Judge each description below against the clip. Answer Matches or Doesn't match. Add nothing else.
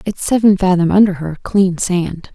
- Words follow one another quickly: Doesn't match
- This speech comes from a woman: Matches